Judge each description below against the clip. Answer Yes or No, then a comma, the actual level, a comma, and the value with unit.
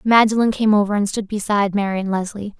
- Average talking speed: Yes, average, 185 wpm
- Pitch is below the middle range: No, high, 205 Hz